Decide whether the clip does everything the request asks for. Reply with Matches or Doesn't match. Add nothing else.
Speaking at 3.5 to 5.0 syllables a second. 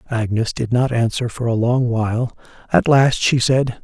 Matches